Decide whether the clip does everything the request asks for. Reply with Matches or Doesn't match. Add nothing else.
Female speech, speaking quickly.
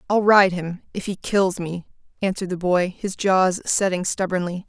Doesn't match